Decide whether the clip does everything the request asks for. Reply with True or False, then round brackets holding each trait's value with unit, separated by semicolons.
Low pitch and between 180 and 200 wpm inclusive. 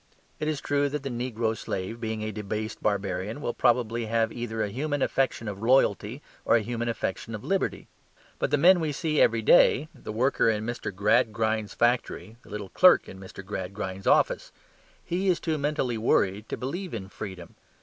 True (115 Hz; 185 wpm)